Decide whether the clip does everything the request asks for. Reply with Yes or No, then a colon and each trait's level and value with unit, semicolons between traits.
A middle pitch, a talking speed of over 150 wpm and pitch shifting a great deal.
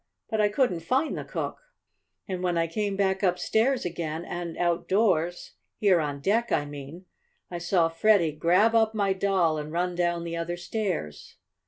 No: medium, 175 Hz; average, 170 wpm; average, 3.4 semitones